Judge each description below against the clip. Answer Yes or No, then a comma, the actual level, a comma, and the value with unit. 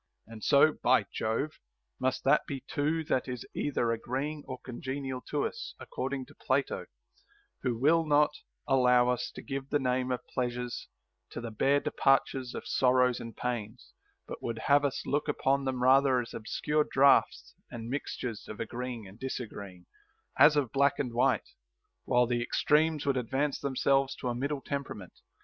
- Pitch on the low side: Yes, low, 130 Hz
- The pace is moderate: Yes, average, 165 wpm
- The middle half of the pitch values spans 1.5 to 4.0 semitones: Yes, narrow, 2.5 semitones